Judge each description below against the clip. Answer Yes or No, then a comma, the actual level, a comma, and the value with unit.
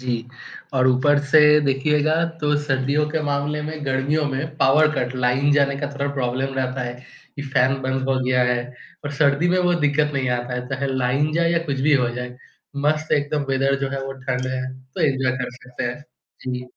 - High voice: No, low, 135 Hz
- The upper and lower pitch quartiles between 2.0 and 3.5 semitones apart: Yes, narrow, 2.4 semitones